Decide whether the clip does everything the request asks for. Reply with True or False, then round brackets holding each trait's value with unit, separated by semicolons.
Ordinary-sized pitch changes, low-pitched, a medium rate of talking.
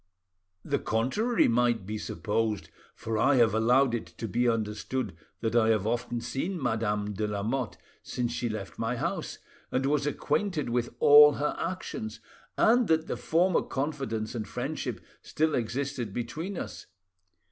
True (4.6 semitones; 120 Hz; 150 wpm)